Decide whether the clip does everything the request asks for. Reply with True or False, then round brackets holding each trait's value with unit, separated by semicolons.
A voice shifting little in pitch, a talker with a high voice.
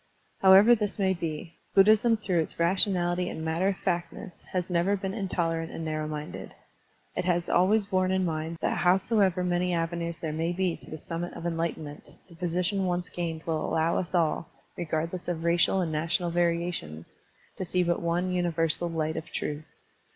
False (2.1 semitones; 175 Hz)